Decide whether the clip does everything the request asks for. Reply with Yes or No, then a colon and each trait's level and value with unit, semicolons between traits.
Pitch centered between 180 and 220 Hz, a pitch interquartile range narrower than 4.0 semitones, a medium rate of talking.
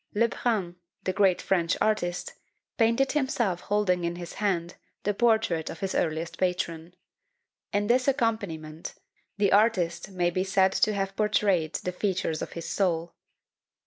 Yes: high, 190 Hz; average, 3.6 semitones; average, 145 wpm